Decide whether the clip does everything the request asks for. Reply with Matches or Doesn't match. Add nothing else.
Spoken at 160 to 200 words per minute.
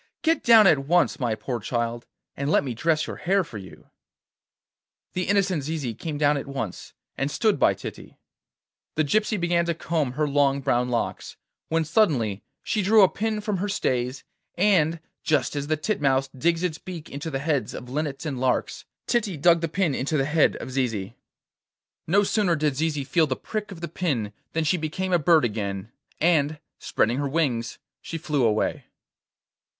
Matches